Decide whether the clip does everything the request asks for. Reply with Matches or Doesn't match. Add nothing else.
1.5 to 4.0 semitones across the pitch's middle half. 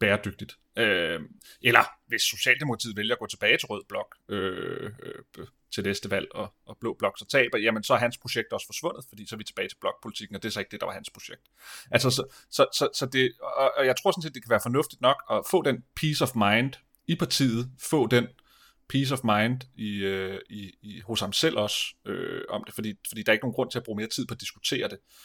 Matches